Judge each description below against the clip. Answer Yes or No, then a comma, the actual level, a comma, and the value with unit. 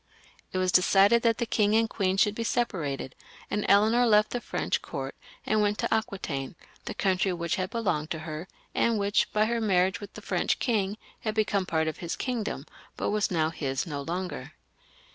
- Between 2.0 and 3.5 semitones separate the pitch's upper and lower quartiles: No, average, 4.2 semitones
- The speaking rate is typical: Yes, average, 195 wpm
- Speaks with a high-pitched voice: Yes, high, 200 Hz